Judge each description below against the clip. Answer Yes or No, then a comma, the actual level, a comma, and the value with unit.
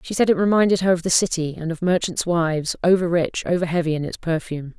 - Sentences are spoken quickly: Yes, fast, 240 wpm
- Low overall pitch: No, medium, 170 Hz